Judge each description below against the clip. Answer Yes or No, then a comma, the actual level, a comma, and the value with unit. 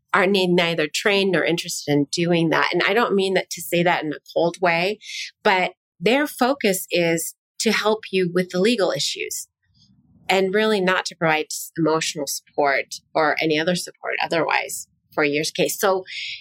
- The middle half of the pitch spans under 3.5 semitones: Yes, average, 3.0 semitones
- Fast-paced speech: No, average, 170 wpm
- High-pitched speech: No, medium, 180 Hz